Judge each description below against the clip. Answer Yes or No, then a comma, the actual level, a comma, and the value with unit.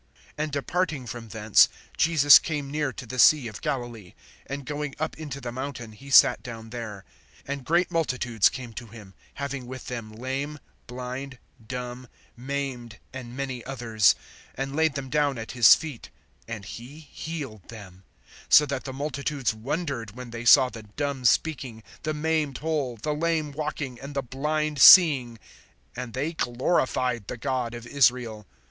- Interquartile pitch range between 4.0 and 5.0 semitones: No, average, 3.6 semitones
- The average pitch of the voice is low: Yes, low, 130 Hz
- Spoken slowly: No, average, 160 wpm